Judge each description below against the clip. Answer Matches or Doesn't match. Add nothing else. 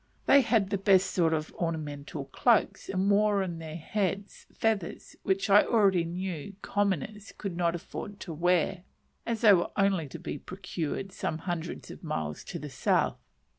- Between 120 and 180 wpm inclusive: Matches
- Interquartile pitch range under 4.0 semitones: Matches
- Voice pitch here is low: Doesn't match